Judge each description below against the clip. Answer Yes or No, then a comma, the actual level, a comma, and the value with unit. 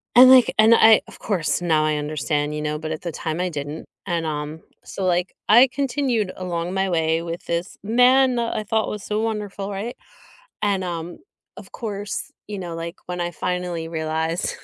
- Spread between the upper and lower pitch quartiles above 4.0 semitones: Yes, average, 4.6 semitones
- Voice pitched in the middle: Yes, medium, 180 Hz